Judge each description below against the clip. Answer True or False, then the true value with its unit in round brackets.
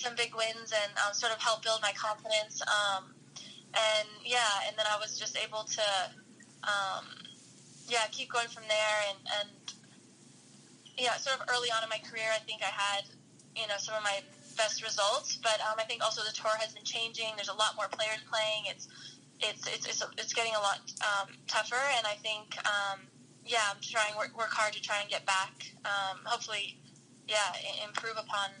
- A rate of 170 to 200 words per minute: True (195 wpm)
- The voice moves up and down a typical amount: False (1.6 semitones)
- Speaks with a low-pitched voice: False (215 Hz)